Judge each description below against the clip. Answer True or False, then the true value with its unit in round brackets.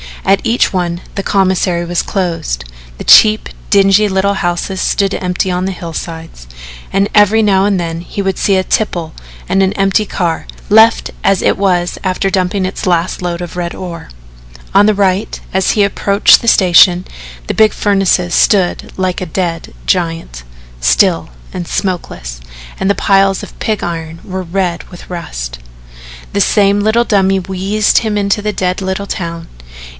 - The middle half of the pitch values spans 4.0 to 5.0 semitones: False (2.4 semitones)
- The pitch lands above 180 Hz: True (190 Hz)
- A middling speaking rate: True (165 wpm)